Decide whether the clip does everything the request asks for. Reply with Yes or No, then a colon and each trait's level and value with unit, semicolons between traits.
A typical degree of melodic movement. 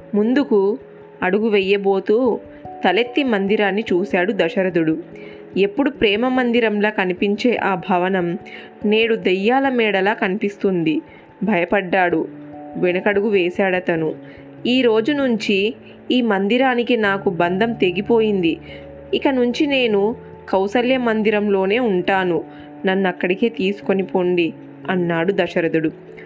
Yes: average, 4.0 semitones